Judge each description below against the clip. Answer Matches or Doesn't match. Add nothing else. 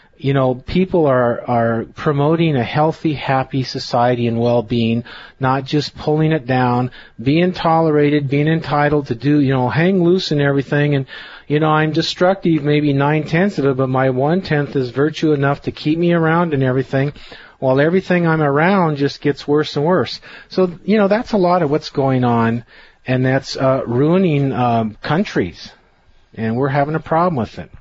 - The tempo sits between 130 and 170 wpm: Doesn't match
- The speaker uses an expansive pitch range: Doesn't match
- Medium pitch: Matches